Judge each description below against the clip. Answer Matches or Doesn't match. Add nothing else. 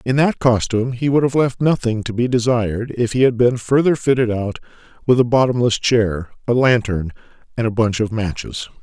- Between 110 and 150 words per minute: Doesn't match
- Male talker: Matches